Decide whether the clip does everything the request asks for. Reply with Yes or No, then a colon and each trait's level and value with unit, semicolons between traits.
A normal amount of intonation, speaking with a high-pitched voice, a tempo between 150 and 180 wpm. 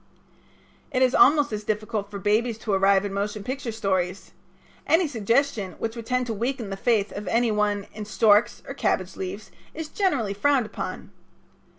Yes: average, 3.7 semitones; high, 215 Hz; average, 175 wpm